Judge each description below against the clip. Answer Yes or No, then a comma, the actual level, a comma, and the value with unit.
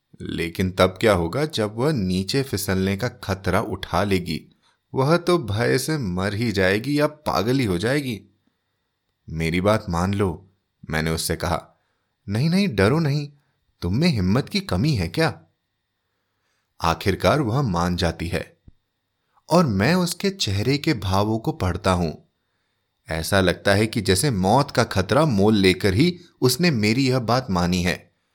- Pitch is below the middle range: Yes, low, 100 Hz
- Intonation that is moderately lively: No, wide, 6.3 semitones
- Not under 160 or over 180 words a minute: No, average, 150 wpm